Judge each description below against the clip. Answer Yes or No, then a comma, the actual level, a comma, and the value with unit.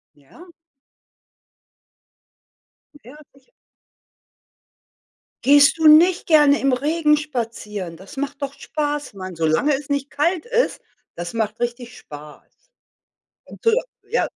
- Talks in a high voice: Yes, very high, 280 Hz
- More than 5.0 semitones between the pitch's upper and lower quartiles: Yes, wide, 5.5 semitones